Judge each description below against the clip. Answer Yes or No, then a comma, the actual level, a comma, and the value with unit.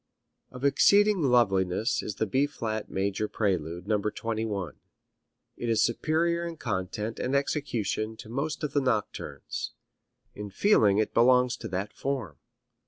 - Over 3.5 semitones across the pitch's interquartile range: Yes, average, 5.3 semitones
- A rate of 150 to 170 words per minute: No, average, 140 wpm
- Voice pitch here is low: Yes, low, 115 Hz